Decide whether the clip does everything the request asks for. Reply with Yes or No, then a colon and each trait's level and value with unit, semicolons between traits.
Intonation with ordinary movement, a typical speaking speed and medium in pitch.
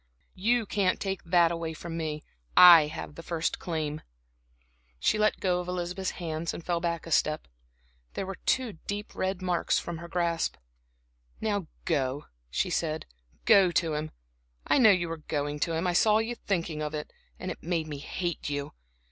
Yes: average, 3.0 semitones; average, 180 wpm; medium, 170 Hz